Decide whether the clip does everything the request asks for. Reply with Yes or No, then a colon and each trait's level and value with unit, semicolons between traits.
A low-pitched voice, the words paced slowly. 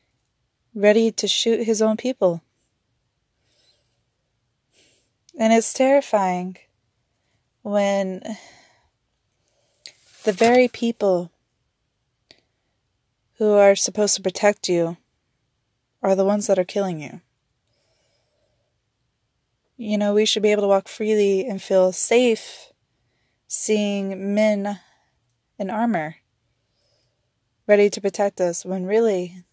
No: high, 190 Hz; slow, 100 wpm